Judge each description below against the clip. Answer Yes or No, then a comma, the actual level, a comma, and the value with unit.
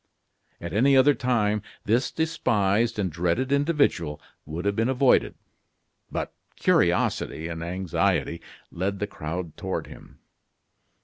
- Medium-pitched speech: No, low, 105 Hz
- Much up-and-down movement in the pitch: Yes, wide, 6.8 semitones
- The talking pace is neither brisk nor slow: No, slow, 120 wpm